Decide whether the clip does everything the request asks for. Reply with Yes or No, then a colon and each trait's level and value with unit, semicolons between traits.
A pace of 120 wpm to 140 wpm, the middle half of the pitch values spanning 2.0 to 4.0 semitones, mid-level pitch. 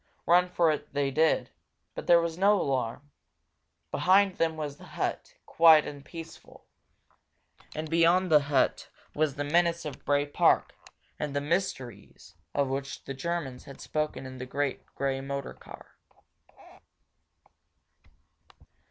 Yes: slow, 135 wpm; average, 3.5 semitones; medium, 150 Hz